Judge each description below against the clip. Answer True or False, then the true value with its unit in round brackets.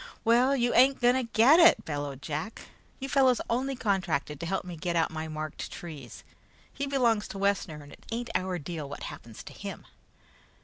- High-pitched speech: True (195 Hz)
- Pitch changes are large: True (8.0 semitones)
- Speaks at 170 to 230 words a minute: True (195 wpm)